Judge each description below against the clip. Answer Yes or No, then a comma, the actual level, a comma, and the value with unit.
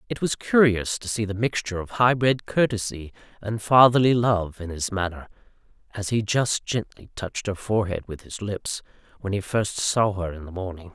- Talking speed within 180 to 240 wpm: Yes, average, 190 wpm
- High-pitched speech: No, low, 105 Hz